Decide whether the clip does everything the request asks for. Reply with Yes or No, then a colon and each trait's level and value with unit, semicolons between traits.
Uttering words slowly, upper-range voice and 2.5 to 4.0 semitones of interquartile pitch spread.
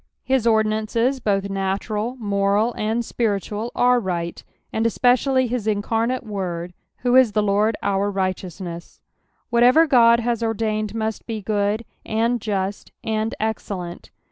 Yes: slow, 130 wpm; high, 220 Hz; average, 2.8 semitones